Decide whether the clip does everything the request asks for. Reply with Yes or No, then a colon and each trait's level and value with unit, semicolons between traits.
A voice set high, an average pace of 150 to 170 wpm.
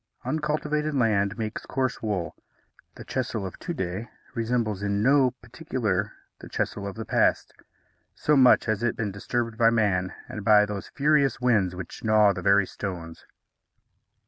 No: low, 110 Hz; average, 155 wpm